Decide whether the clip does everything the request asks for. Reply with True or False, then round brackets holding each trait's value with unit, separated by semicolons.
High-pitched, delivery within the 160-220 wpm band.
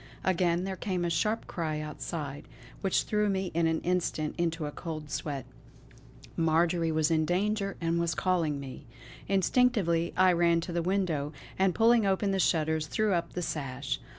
False (170 Hz; 170 wpm)